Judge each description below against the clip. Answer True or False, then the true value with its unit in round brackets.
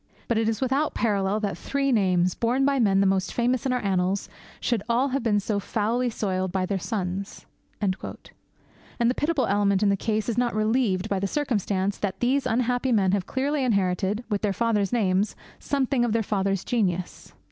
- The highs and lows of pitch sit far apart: False (4.0 semitones)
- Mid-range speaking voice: False (215 Hz)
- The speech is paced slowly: False (190 wpm)